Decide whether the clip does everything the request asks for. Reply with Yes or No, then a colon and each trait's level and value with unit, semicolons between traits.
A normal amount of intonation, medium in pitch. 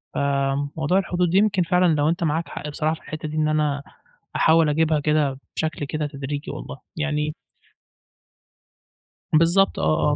No: narrow, 2.1 semitones; medium, 155 Hz